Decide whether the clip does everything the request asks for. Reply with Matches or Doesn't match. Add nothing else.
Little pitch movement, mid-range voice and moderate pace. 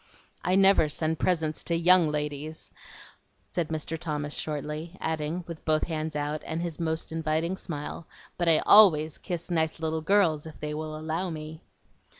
Matches